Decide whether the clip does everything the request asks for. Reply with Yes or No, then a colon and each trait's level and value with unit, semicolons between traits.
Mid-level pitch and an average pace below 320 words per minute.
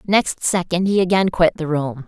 Yes: medium, 175 Hz; average, 200 wpm